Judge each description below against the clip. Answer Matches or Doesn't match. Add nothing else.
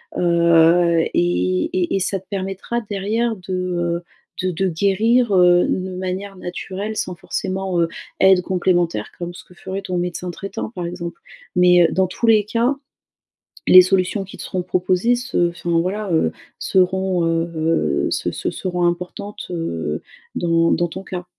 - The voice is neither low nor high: Matches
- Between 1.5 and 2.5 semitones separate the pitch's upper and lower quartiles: Matches